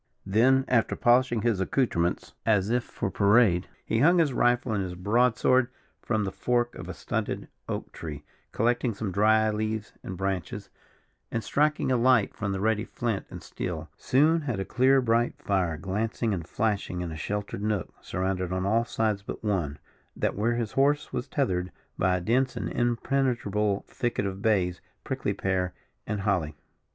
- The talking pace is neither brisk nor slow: Yes, average, 175 wpm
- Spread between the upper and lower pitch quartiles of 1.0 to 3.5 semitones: No, average, 4.1 semitones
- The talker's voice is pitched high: No, low, 110 Hz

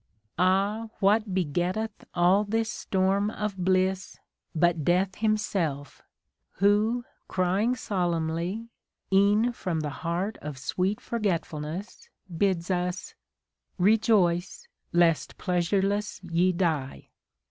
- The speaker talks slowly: Yes, slow, 95 wpm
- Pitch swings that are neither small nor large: Yes, average, 3.2 semitones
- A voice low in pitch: No, medium, 185 Hz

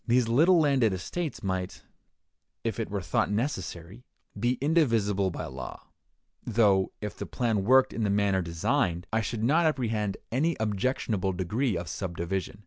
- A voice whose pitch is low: Yes, low, 105 Hz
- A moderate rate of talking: Yes, average, 150 wpm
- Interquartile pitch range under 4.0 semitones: No, average, 5.1 semitones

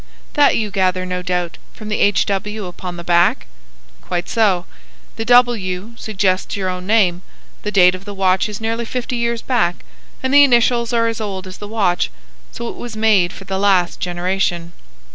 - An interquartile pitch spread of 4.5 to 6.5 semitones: No, average, 3.7 semitones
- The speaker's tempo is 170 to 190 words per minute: Yes, average, 185 wpm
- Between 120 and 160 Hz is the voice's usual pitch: No, high, 200 Hz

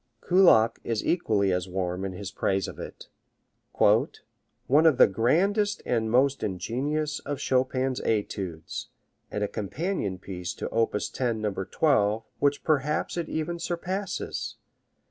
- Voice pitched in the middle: No, low, 120 Hz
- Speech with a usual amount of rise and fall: No, wide, 7.5 semitones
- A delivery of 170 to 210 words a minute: No, slow, 135 wpm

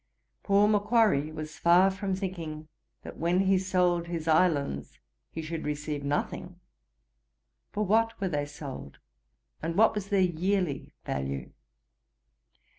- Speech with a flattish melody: No, average, 4.2 semitones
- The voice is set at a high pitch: No, medium, 170 Hz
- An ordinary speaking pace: No, slow, 125 wpm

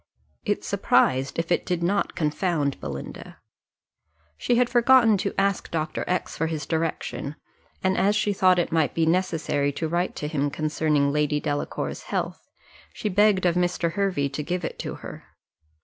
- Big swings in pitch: No, average, 3.9 semitones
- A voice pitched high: No, medium, 165 Hz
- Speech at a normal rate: Yes, average, 165 wpm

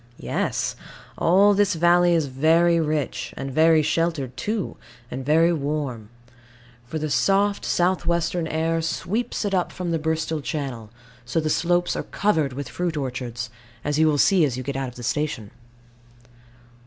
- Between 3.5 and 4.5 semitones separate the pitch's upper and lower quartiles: Yes, average, 4.0 semitones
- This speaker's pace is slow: No, average, 165 wpm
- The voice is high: No, medium, 160 Hz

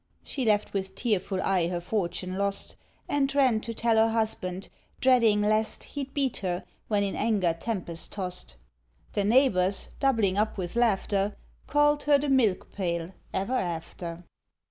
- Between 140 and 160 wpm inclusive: Yes, average, 150 wpm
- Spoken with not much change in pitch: No, average, 4.4 semitones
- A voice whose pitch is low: No, high, 205 Hz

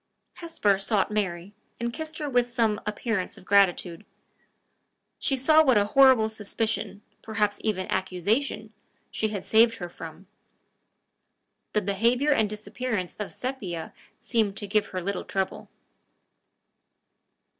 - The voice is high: Yes, high, 215 Hz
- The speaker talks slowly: Yes, slow, 125 wpm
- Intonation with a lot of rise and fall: No, average, 3.4 semitones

